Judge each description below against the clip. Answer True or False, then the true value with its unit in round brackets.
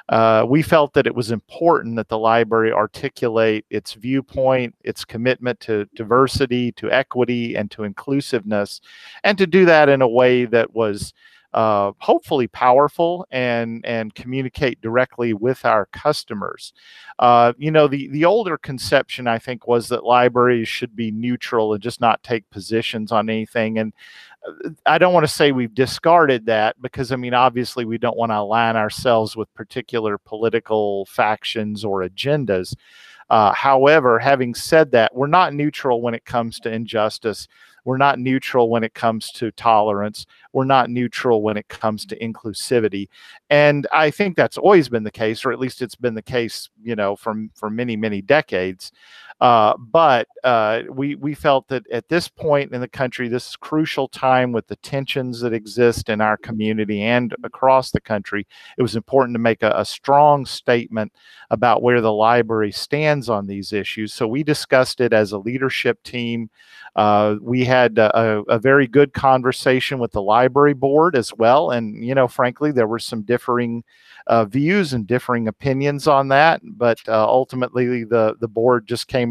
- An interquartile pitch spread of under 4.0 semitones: True (3.1 semitones)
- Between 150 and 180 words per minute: True (175 wpm)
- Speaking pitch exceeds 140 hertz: False (120 Hz)